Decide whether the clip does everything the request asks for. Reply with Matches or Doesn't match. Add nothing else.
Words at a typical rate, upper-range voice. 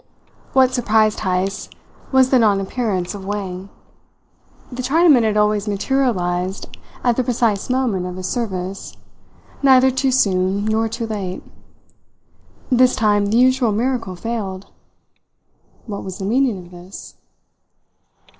Doesn't match